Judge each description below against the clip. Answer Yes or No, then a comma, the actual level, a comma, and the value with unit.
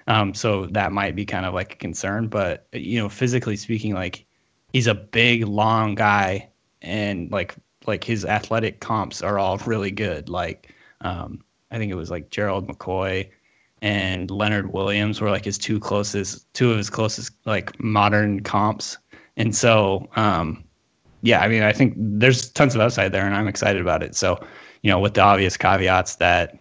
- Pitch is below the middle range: Yes, low, 105 Hz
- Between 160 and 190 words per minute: Yes, average, 185 wpm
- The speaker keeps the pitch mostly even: Yes, narrow, 2.1 semitones